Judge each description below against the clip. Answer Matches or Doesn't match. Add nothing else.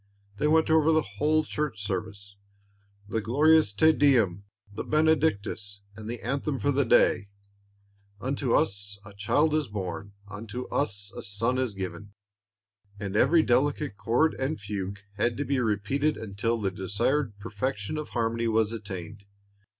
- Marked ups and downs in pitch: Matches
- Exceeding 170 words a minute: Doesn't match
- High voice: Doesn't match